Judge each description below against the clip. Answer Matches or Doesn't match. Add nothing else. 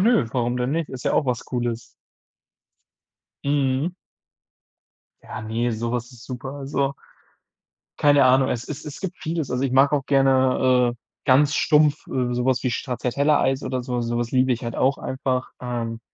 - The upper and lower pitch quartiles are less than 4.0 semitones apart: Matches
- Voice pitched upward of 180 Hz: Doesn't match